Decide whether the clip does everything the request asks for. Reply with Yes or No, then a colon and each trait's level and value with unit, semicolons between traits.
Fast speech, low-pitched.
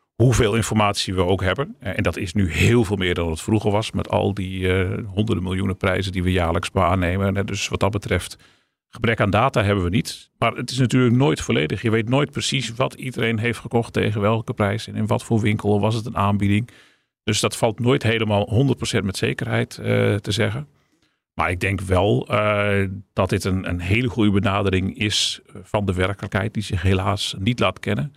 Yes: fast, 205 wpm; low, 105 Hz